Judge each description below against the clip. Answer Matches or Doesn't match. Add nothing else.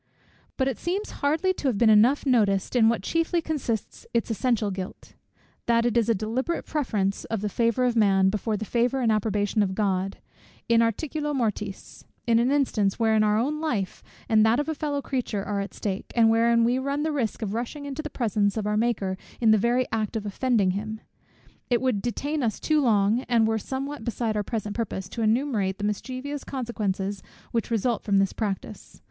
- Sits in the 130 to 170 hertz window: Doesn't match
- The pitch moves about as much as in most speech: Matches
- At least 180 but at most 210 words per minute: Matches